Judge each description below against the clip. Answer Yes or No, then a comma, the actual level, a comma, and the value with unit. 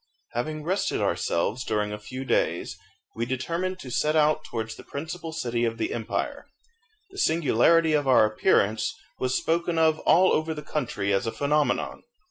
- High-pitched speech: No, medium, 140 Hz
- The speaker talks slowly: No, average, 165 wpm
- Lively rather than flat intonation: Yes, wide, 5.7 semitones